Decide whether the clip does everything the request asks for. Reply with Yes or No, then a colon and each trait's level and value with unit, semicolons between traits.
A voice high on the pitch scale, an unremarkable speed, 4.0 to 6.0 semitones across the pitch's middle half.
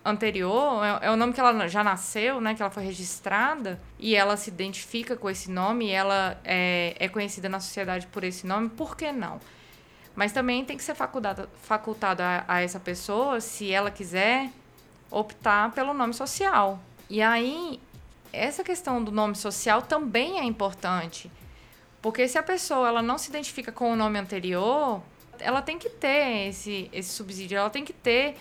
Yes: high, 215 Hz; average, 175 wpm; average, 4.6 semitones